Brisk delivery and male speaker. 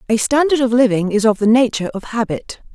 No: fast, 220 wpm; female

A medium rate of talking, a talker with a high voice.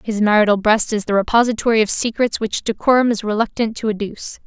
Yes: average, 190 wpm; high, 215 Hz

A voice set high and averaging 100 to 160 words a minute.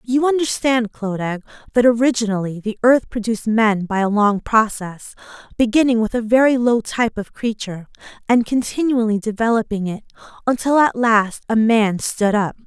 Yes: high, 225 Hz; average, 150 wpm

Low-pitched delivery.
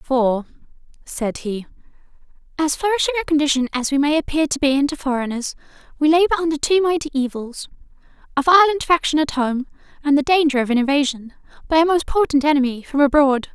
No: very high, 290 Hz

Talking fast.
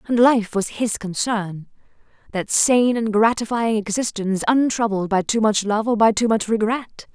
No: average, 170 wpm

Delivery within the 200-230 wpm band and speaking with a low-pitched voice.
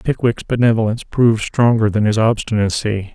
No: slow, 135 wpm; low, 110 Hz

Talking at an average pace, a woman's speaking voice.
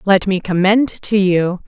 Yes: average, 180 wpm; female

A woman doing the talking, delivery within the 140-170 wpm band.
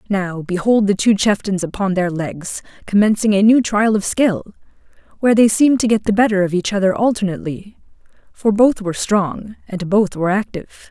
No: female; average, 180 wpm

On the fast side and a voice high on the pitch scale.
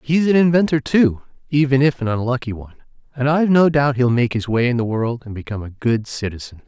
No: fast, 225 wpm; low, 130 Hz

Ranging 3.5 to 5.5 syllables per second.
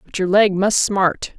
Yes: 4.0 syllables/s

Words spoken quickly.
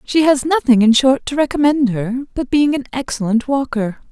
No: average, 190 wpm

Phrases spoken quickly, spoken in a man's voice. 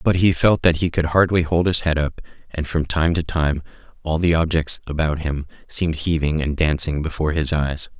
Yes: fast, 210 wpm; male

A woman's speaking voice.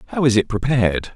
No: male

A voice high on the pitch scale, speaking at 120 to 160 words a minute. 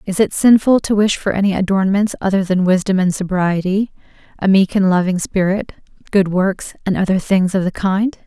No: high, 195 Hz; average, 190 wpm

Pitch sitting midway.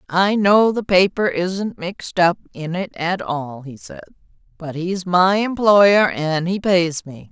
Yes: medium, 180 Hz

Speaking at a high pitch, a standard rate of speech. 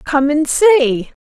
Yes: very high, 295 Hz; average, 145 wpm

